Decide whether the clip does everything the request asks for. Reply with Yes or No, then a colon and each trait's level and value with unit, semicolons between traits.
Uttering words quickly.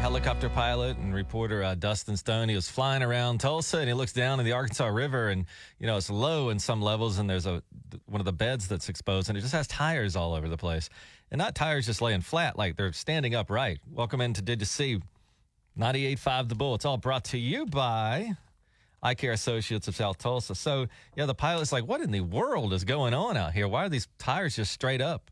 Yes: fast, 230 wpm